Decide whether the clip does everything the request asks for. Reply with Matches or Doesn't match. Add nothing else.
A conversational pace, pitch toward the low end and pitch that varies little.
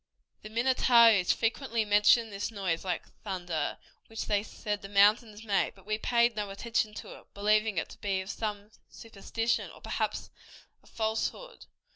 Doesn't match